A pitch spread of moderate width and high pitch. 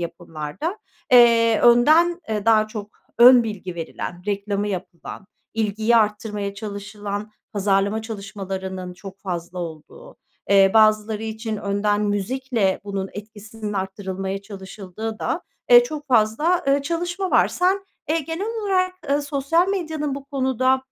No: wide, 5.7 semitones; high, 215 Hz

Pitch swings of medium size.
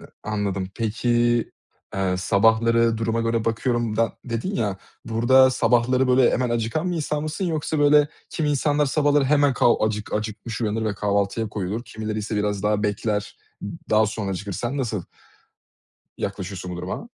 Yes: average, 3.7 semitones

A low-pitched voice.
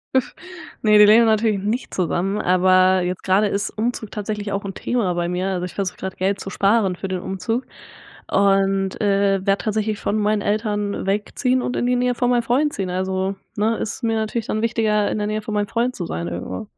No: high, 205 Hz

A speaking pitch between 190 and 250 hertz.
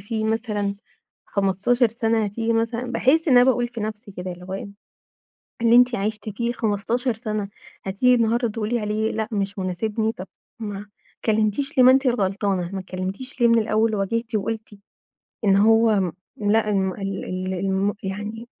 Yes: high, 215 Hz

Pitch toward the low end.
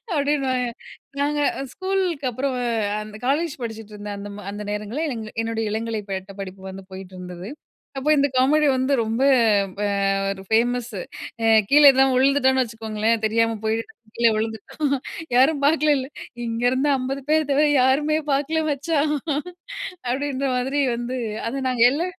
No: very high, 255 Hz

